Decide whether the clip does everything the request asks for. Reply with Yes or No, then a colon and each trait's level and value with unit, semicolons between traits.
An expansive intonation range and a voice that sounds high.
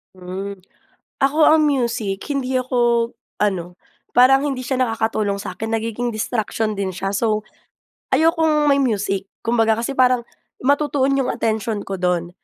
No: average, 4.4 semitones; high, 230 Hz